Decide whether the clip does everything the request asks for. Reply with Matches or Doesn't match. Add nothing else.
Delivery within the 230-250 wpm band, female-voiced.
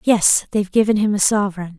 Doesn't match